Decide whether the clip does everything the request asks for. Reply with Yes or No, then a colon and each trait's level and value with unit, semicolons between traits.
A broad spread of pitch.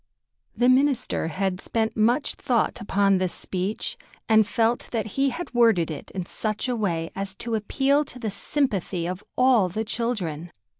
No: average, 4.5 semitones